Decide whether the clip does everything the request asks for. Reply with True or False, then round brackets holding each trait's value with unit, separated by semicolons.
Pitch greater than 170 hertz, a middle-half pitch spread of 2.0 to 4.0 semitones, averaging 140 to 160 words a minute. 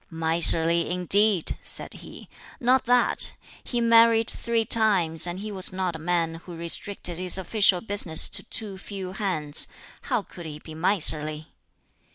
False (185 Hz; 4.4 semitones; 150 wpm)